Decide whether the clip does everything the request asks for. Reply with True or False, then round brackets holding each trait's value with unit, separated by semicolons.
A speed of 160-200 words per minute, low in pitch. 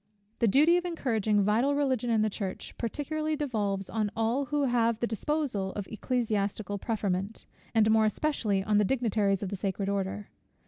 False (170 wpm; 220 Hz)